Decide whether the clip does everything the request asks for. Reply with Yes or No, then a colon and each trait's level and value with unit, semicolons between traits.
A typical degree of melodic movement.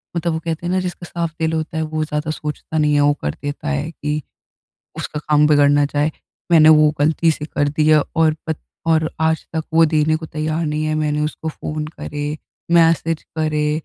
No: narrow, 1.1 semitones